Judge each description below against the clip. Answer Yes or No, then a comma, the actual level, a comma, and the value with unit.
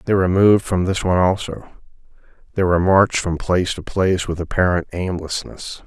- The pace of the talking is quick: No, average, 175 wpm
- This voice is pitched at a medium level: No, very low, 90 Hz